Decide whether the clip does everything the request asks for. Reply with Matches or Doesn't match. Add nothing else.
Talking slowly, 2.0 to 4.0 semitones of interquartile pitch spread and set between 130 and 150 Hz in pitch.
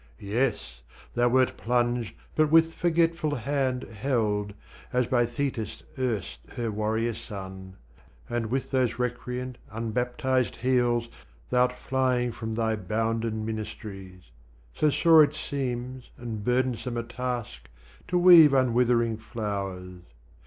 Doesn't match